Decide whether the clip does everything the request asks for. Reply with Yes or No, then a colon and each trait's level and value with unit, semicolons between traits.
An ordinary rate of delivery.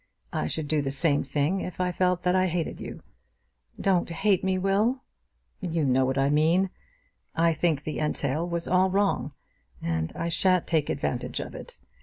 Yes: average, 180 wpm